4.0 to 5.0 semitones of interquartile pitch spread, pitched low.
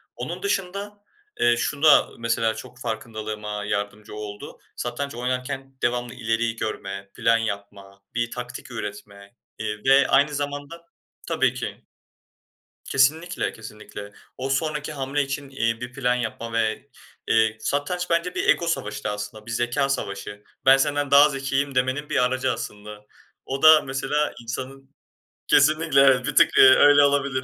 Yes: average, 4.3 semitones; low, 125 Hz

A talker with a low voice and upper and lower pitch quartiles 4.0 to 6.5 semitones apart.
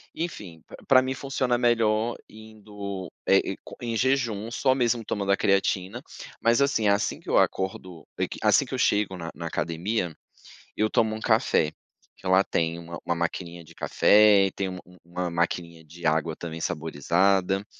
Yes: low, 100 Hz; average, 4.5 semitones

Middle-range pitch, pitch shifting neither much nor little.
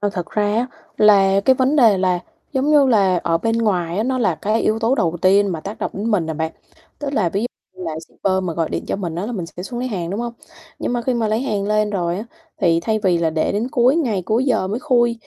No: high, 210 Hz; average, 4.7 semitones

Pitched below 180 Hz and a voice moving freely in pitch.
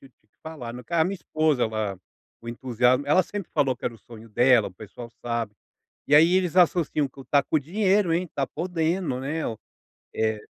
Yes: medium, 140 Hz; wide, 6.0 semitones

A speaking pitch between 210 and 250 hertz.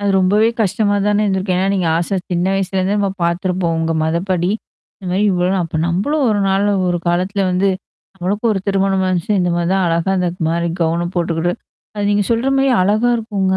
No: high, 190 Hz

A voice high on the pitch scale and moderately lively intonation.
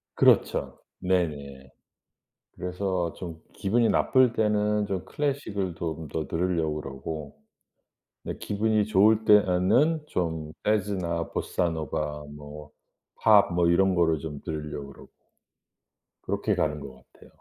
No: very low, 90 Hz; average, 5.0 semitones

